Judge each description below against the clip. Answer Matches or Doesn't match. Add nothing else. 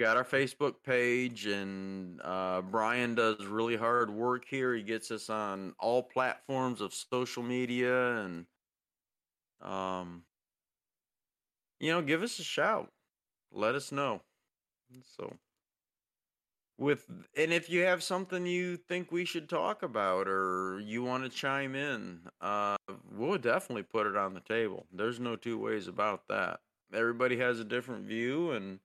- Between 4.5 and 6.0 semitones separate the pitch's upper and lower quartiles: Matches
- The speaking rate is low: Doesn't match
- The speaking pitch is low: Matches